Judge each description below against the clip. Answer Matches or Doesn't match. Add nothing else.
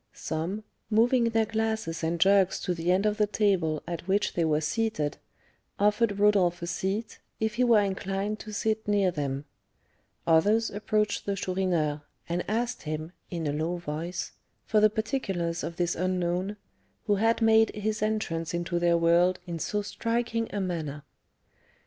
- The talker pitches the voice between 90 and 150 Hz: Doesn't match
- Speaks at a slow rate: Doesn't match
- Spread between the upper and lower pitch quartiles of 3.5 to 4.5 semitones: Matches